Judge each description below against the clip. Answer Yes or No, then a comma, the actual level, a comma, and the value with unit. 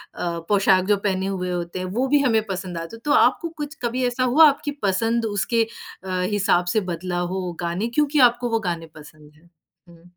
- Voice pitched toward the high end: Yes, high, 195 Hz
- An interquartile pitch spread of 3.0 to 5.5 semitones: Yes, average, 5.0 semitones